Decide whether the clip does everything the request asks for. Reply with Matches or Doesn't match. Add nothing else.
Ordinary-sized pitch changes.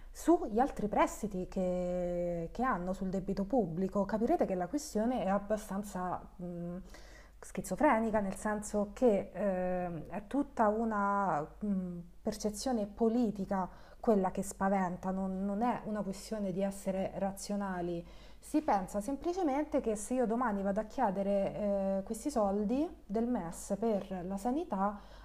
Matches